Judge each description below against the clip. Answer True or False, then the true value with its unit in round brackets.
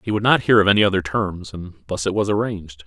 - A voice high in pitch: False (95 Hz)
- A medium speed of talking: False (270 wpm)